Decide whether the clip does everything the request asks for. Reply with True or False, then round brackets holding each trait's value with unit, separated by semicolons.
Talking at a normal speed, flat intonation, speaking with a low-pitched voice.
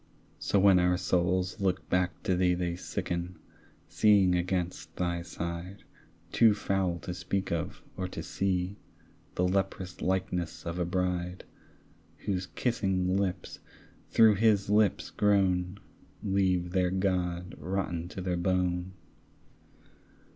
False (125 wpm; 1.5 semitones; 90 Hz)